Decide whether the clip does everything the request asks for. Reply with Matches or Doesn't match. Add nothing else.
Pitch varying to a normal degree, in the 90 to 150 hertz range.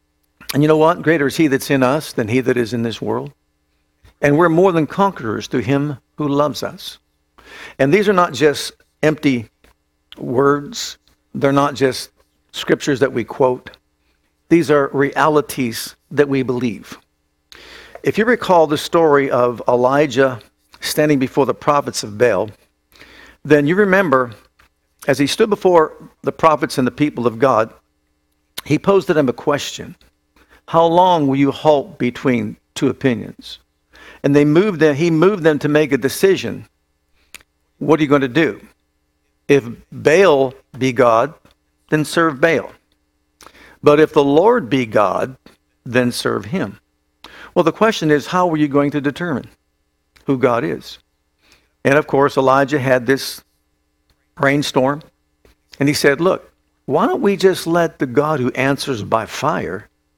Matches